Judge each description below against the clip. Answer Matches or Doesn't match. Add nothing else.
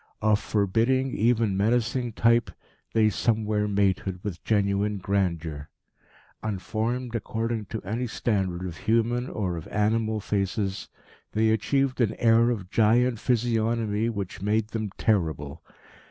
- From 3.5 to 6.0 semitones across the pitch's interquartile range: Doesn't match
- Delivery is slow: Matches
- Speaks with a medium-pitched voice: Doesn't match